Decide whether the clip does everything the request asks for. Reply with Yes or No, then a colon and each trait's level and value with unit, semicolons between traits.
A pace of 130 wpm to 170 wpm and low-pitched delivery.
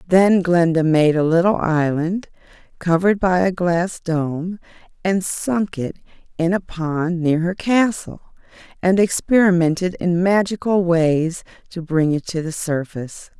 No: average, 140 wpm; medium, 175 Hz